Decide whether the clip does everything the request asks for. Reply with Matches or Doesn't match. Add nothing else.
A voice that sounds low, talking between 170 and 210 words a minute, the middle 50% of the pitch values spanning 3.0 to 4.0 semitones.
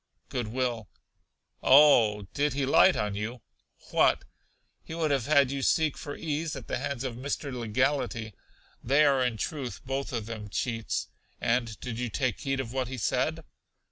Matches